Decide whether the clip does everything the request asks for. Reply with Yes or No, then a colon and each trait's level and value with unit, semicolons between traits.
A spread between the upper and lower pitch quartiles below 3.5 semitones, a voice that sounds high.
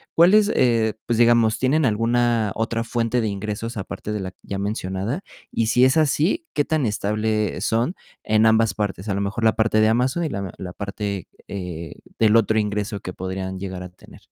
No: average, 3.0 semitones; low, 110 Hz